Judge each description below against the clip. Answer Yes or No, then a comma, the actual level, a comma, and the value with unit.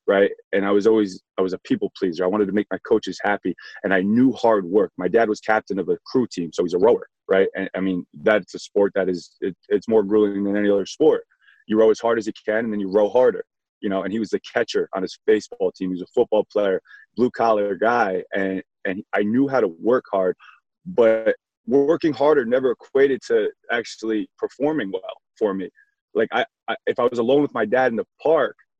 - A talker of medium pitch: No, low, 115 Hz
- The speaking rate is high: Yes, fast, 240 wpm